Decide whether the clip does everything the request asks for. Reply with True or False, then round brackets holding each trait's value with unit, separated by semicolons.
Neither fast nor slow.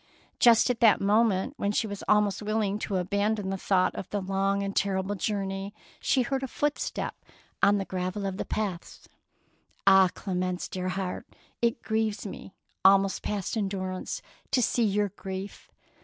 True (165 wpm)